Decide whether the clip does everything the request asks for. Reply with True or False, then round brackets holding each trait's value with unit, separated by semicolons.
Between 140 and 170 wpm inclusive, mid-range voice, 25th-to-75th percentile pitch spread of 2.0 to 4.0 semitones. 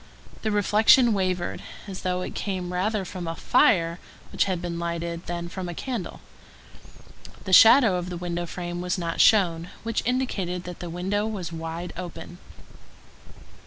True (160 wpm; 180 Hz; 3.0 semitones)